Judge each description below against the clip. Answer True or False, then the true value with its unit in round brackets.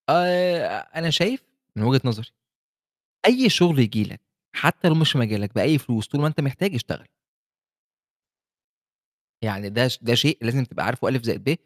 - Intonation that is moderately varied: False (6.2 semitones)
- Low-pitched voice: True (130 Hz)